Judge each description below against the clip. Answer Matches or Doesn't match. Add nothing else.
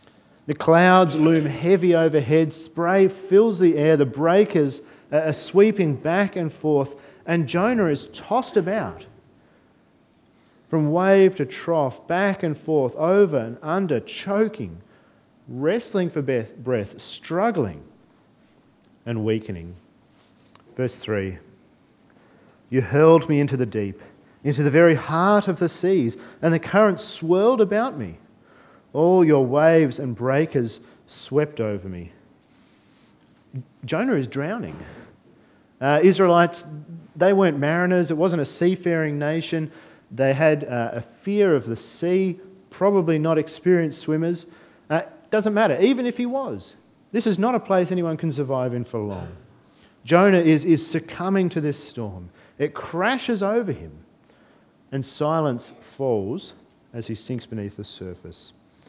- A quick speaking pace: Doesn't match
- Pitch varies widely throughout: Matches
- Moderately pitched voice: Matches